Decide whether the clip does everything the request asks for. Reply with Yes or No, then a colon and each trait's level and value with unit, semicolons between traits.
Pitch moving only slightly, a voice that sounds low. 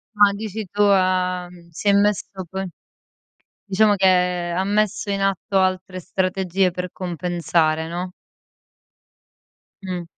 No: narrow, 1.9 semitones; medium, 185 Hz